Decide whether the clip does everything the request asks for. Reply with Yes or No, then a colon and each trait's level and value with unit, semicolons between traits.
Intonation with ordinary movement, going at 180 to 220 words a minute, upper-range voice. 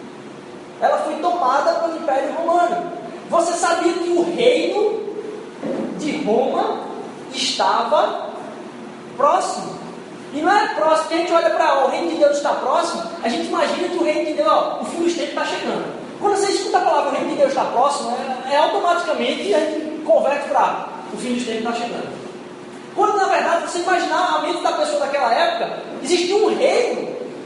Yes: average, 3.0 semitones; fast, 185 wpm; very high, 335 Hz